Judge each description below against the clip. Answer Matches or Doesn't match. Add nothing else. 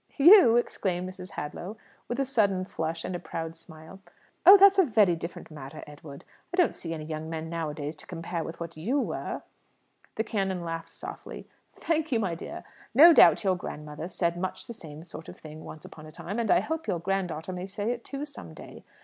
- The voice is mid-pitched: Matches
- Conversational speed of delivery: Doesn't match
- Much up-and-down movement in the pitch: Matches